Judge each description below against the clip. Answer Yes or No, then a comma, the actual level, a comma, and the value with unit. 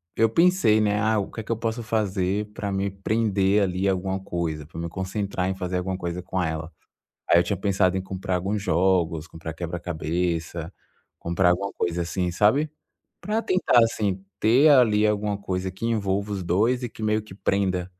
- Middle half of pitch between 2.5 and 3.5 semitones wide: Yes, average, 3.1 semitones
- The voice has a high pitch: No, very low, 95 Hz